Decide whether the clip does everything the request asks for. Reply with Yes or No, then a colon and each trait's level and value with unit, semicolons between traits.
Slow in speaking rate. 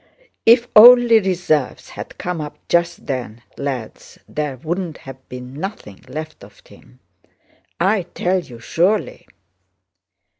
Yes: slow, 120 wpm